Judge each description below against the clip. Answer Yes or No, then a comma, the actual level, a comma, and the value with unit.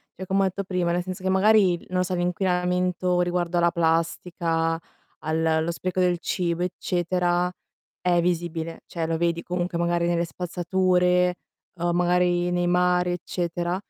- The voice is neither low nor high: Yes, medium, 175 Hz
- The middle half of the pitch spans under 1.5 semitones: Yes, narrow, 1.0 semitones